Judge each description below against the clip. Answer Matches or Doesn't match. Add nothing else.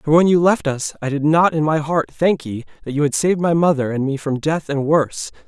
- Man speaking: Matches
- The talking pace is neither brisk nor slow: Doesn't match